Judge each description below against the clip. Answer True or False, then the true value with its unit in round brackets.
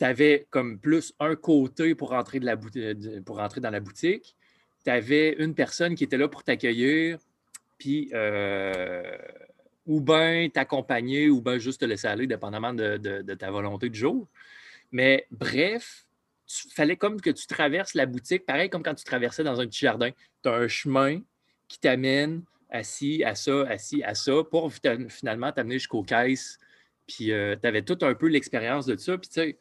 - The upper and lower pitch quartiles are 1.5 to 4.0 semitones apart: False (4.8 semitones)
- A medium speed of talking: True (195 wpm)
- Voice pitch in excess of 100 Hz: True (135 Hz)